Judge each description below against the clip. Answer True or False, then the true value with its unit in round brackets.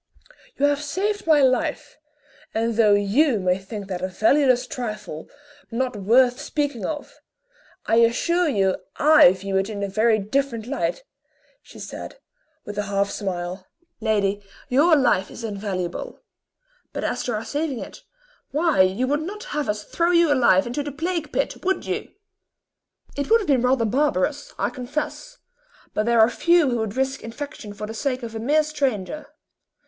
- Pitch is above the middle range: True (245 Hz)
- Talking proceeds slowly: False (170 wpm)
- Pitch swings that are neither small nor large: False (5.9 semitones)